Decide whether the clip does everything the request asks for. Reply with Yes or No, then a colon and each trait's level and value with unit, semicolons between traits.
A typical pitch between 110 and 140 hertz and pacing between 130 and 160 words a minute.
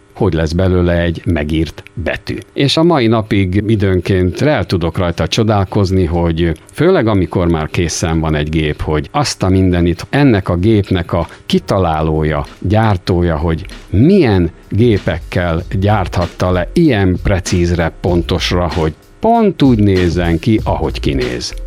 No: very low, 90 Hz; average, 135 wpm